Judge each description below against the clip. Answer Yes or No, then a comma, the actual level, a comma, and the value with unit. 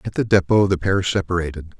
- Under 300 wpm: Yes, average, 200 wpm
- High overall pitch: No, very low, 90 Hz